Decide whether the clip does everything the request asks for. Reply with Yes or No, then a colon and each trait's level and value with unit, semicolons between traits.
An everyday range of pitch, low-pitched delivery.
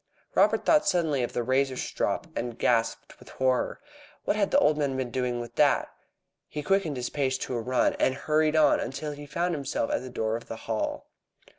Yes: average, 3.9 semitones; low, 130 Hz